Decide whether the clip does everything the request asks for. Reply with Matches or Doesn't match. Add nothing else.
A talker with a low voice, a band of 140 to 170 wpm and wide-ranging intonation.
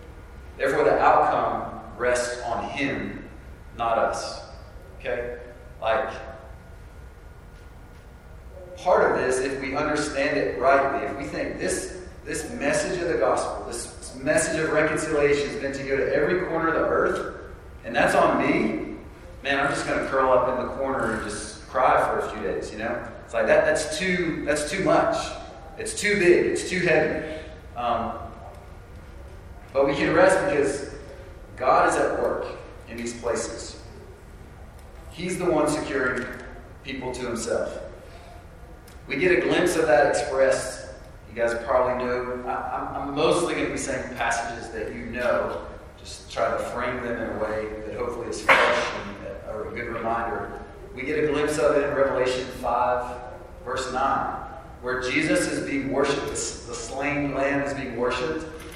Matches